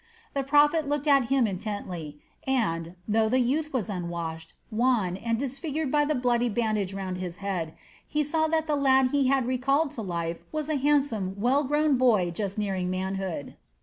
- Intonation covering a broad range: Yes, wide, 6.8 semitones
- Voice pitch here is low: No, high, 240 Hz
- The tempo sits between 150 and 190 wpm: Yes, average, 180 wpm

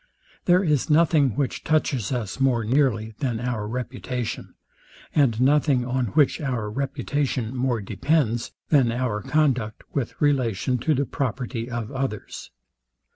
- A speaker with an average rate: No, slow, 130 wpm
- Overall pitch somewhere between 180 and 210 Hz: No, low, 125 Hz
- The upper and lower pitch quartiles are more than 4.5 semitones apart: No, average, 3.5 semitones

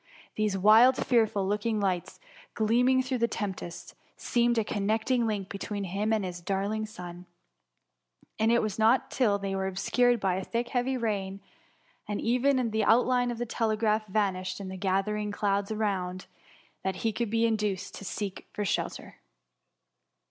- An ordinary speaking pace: Yes, average, 165 wpm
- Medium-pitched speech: No, high, 210 Hz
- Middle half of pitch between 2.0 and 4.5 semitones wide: Yes, average, 2.9 semitones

